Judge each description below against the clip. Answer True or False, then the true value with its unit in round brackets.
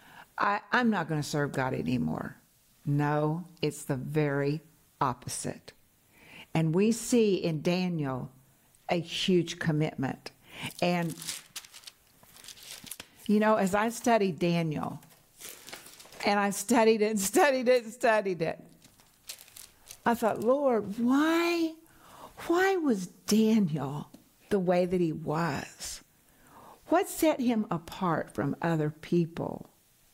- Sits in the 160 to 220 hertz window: True (185 Hz)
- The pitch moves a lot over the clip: True (6.4 semitones)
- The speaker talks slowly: True (115 wpm)